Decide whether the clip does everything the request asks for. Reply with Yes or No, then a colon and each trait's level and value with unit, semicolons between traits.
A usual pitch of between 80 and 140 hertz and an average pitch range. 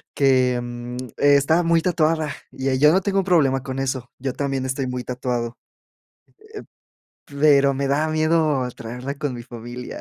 Yes: low, 135 Hz; average, 3.5 semitones